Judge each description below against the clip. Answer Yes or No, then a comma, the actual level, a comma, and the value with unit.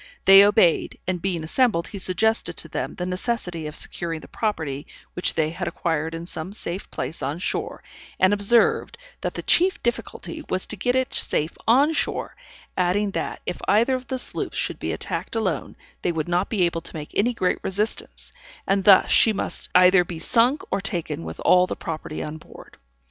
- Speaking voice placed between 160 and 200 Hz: Yes, medium, 185 Hz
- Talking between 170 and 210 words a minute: Yes, average, 190 wpm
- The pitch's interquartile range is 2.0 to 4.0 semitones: No, average, 4.8 semitones